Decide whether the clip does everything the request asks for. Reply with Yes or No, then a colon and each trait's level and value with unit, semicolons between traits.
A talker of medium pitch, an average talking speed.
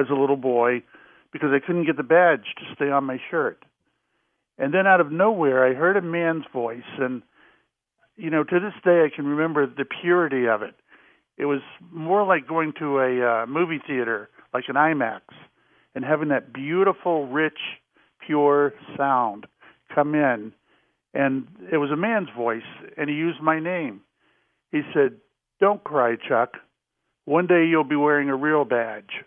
Yes: medium, 150 Hz; average, 170 wpm